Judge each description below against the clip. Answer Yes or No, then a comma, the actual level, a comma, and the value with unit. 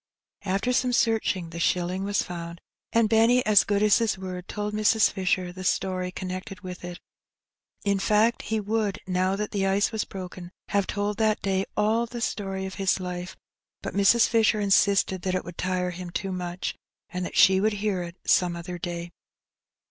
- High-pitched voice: Yes, high, 195 Hz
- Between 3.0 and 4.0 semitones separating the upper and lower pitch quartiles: No, narrow, 2.5 semitones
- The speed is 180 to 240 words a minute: Yes, average, 185 wpm